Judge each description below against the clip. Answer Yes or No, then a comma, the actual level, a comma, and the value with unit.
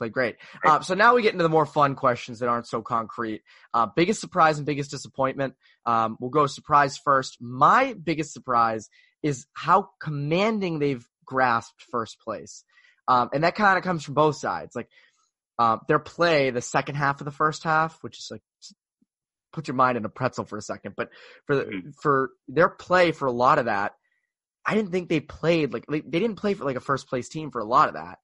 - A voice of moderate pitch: Yes, medium, 145 Hz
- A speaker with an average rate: No, fast, 215 wpm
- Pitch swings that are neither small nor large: Yes, average, 4.9 semitones